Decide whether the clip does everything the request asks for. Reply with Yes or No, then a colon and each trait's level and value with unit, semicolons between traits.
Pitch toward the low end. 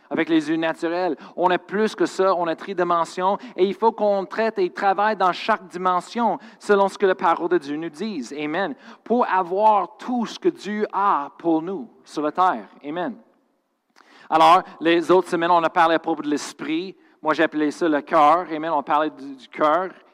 No: medium, 185 Hz